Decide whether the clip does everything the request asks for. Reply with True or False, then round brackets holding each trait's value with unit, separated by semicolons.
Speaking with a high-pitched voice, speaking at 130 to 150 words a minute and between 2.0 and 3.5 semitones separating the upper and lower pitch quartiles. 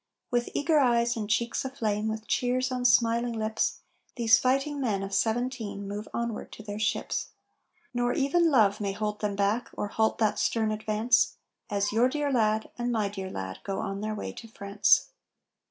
False (220 Hz; 180 wpm; 2.8 semitones)